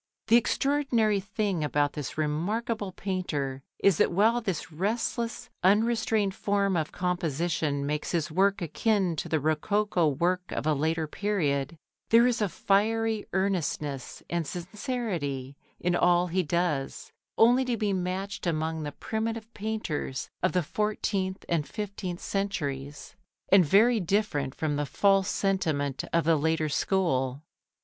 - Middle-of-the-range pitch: Yes, medium, 180 Hz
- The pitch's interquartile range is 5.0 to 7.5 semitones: Yes, average, 5.3 semitones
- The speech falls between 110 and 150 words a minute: Yes, average, 140 wpm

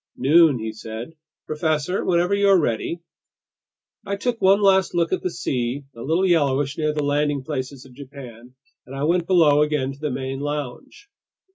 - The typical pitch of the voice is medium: Yes, medium, 150 Hz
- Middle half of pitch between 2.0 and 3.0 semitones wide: No, average, 4.5 semitones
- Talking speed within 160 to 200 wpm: Yes, average, 175 wpm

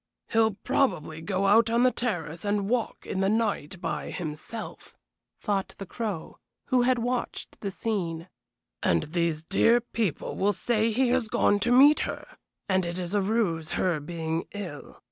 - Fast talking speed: No, average, 165 wpm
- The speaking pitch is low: No, high, 200 Hz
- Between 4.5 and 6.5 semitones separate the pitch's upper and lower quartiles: Yes, average, 5.1 semitones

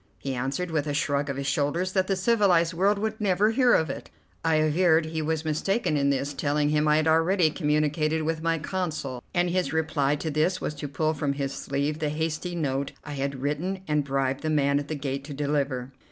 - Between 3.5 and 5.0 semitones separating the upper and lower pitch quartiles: No, average, 2.8 semitones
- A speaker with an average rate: No, fast, 220 wpm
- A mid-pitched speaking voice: Yes, medium, 155 Hz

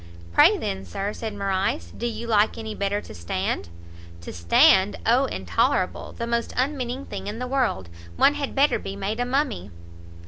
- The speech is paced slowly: No, average, 175 wpm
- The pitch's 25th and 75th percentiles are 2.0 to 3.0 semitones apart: No, average, 4.7 semitones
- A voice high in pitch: Yes, high, 215 Hz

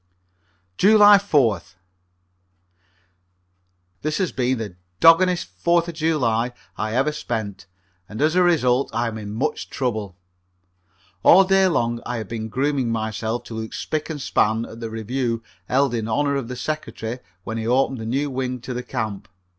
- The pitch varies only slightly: No, average, 5.2 semitones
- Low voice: Yes, low, 125 Hz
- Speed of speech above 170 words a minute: No, average, 160 wpm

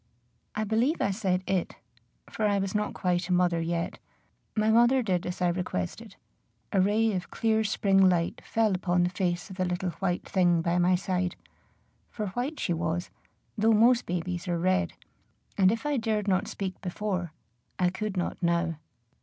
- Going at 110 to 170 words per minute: No, average, 180 wpm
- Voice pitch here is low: No, medium, 185 Hz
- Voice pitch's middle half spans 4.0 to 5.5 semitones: No, average, 3.3 semitones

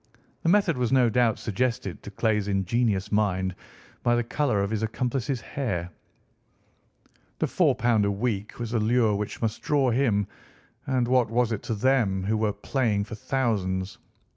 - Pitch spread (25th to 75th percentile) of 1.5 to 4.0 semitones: Yes, average, 3.6 semitones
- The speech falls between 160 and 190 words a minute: Yes, average, 165 wpm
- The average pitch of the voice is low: Yes, low, 115 Hz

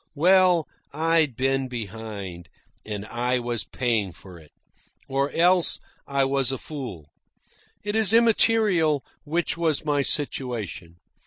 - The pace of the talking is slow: Yes, slow, 120 wpm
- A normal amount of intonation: No, wide, 6.7 semitones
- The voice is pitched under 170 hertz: Yes, low, 135 Hz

